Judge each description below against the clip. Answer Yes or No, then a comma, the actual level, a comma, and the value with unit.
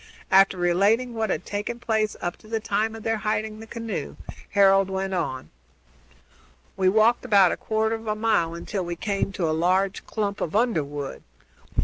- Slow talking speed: No, average, 175 wpm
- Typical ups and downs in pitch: Yes, average, 3.1 semitones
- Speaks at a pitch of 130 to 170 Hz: No, high, 205 Hz